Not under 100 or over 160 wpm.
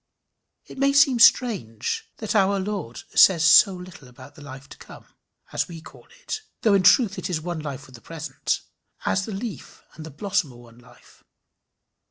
No: average, 190 wpm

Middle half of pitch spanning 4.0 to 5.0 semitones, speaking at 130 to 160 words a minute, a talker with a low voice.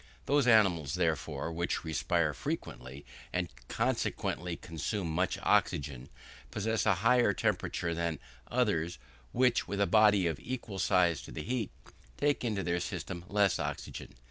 Yes: average, 4.7 semitones; average, 140 wpm; very low, 90 Hz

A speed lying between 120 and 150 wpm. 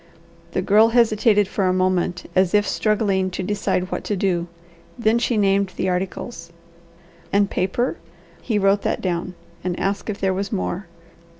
No: average, 165 wpm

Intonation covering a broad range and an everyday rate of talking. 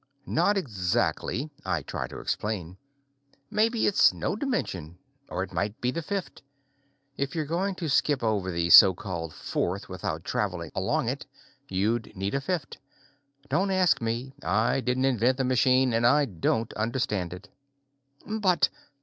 Yes: wide, 7.8 semitones; average, 150 wpm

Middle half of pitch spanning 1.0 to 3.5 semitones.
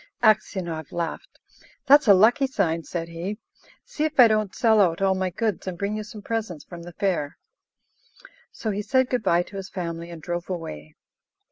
No: average, 4.3 semitones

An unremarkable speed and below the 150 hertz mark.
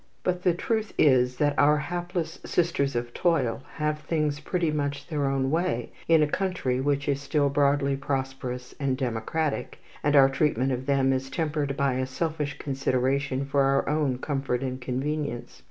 Yes: average, 170 wpm; medium, 140 Hz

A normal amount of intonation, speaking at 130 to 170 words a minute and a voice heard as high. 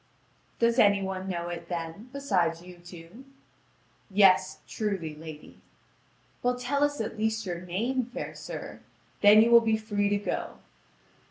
Yes: average, 4.7 semitones; average, 150 wpm; high, 205 Hz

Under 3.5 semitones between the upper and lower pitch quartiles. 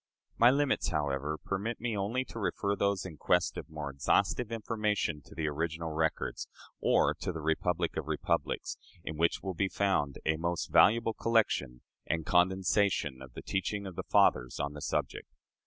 No: average, 4.9 semitones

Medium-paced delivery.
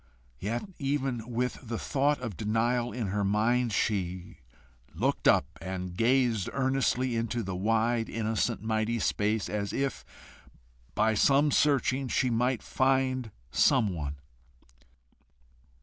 No: slow, 120 wpm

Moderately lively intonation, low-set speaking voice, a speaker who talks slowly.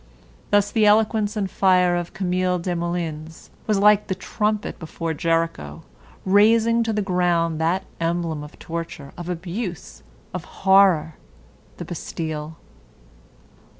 No: average, 3.6 semitones; medium, 180 Hz; slow, 120 wpm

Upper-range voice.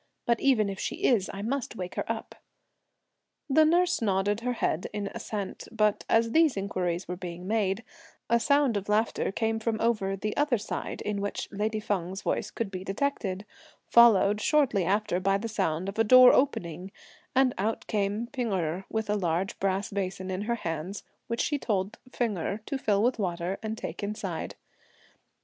Yes: high, 210 Hz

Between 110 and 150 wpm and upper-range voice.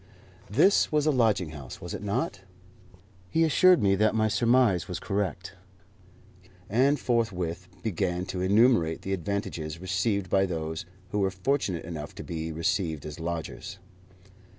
No: average, 145 wpm; very low, 95 Hz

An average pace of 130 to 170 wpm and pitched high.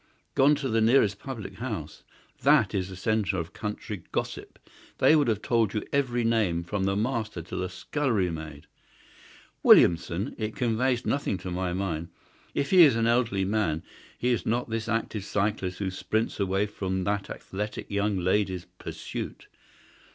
No: average, 165 wpm; low, 105 Hz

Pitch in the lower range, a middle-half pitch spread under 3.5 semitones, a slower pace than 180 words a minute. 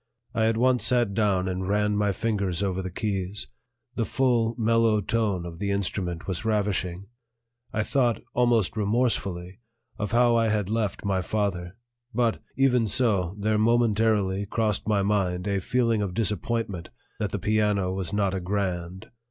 Yes: low, 105 Hz; average, 3.1 semitones; average, 160 wpm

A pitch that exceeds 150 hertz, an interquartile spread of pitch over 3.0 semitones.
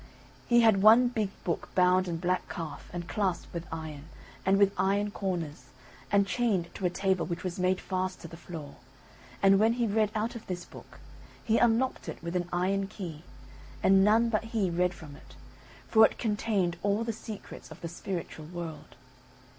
Yes: high, 190 Hz; average, 3.6 semitones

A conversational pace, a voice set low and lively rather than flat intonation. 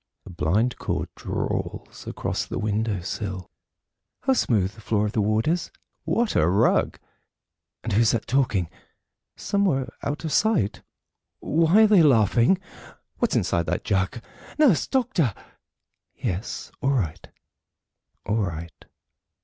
No: slow, 130 wpm; low, 115 Hz; wide, 8.4 semitones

